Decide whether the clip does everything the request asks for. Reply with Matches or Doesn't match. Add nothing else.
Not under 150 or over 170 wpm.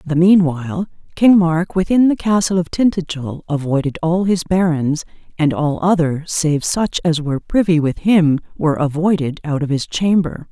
Matches